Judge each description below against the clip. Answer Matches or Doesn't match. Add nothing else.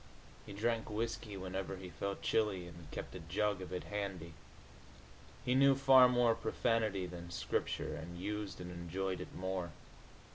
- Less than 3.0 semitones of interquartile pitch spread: Doesn't match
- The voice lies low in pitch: Matches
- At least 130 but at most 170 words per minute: Matches